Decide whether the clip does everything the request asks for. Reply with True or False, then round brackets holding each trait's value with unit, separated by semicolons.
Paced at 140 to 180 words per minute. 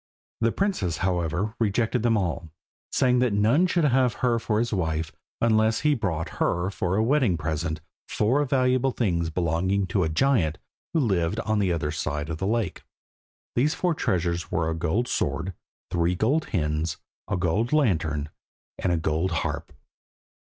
True (165 wpm)